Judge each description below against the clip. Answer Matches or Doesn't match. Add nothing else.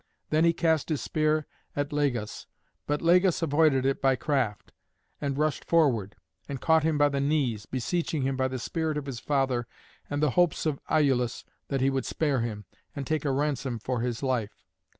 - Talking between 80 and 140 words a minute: Doesn't match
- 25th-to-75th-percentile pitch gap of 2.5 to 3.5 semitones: Matches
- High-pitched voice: Doesn't match